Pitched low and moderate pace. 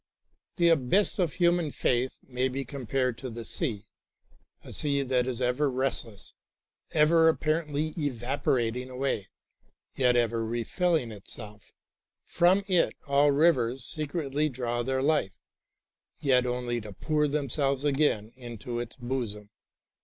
No: low, 130 Hz; slow, 125 wpm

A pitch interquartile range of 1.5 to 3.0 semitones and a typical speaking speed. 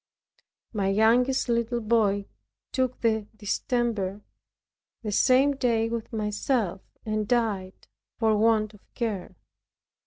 No: narrow, 2.4 semitones; slow, 105 wpm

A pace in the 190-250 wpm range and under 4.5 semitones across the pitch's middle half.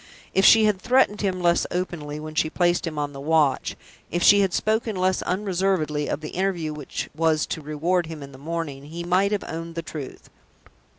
Yes: average, 200 wpm; average, 3.5 semitones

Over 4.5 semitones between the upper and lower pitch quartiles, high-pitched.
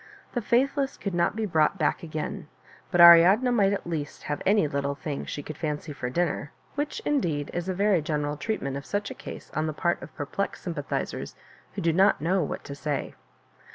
No: average, 5.2 semitones; medium, 170 Hz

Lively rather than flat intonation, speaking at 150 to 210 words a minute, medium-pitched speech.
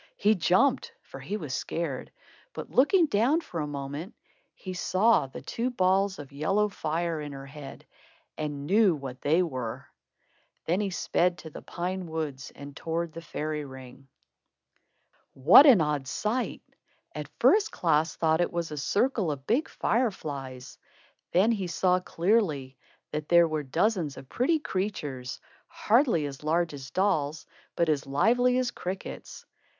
Yes: wide, 6.0 semitones; average, 155 wpm; medium, 165 Hz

